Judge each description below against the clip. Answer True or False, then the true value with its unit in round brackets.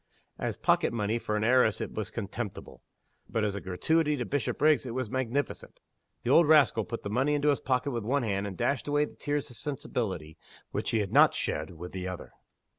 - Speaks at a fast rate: True (210 wpm)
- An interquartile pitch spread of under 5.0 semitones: False (5.6 semitones)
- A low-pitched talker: True (120 Hz)